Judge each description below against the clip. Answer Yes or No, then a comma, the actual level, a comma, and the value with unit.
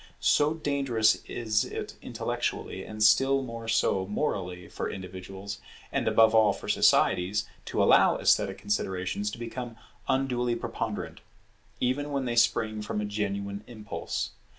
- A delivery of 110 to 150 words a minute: Yes, slow, 135 wpm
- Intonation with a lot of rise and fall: No, average, 3.3 semitones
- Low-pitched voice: Yes, low, 110 Hz